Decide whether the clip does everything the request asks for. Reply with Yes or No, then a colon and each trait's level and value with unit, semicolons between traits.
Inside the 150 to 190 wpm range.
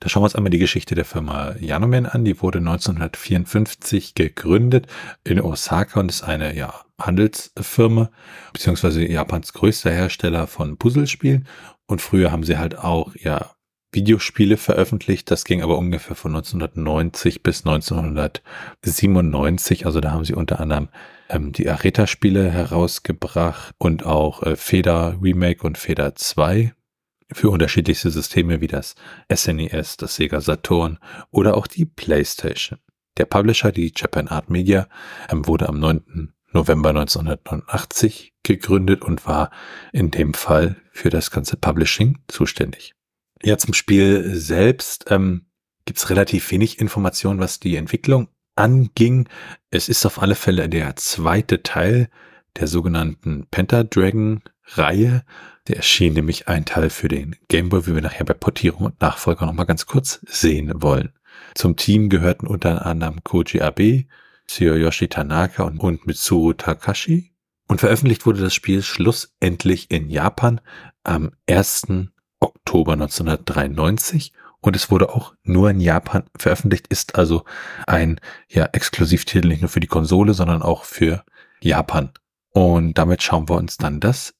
No: average, 140 wpm